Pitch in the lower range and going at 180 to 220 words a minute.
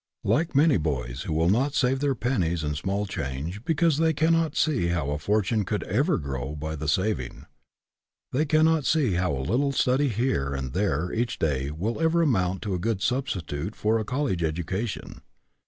Yes: low, 100 Hz; average, 190 wpm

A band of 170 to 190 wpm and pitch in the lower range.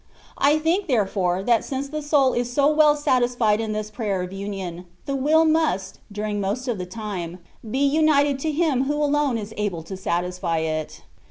No: average, 185 wpm; high, 235 Hz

